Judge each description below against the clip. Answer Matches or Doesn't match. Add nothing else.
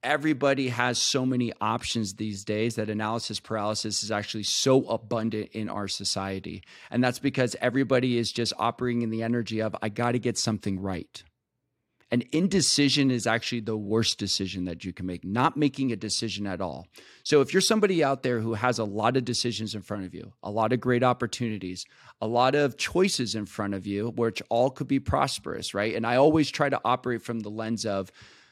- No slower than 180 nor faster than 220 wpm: Matches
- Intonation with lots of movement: Doesn't match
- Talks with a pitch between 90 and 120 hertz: Matches